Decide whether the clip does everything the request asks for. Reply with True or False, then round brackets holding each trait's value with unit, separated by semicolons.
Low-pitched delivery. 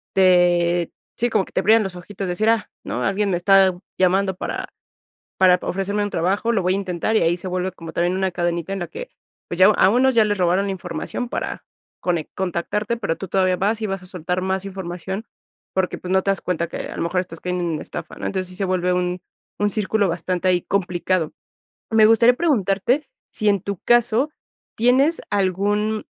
False (190 Hz)